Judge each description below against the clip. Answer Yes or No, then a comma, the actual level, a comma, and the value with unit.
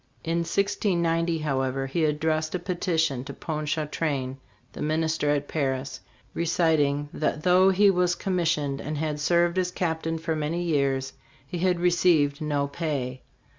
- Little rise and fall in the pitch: No, average, 3.0 semitones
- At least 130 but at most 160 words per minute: Yes, average, 145 wpm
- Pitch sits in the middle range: Yes, medium, 160 Hz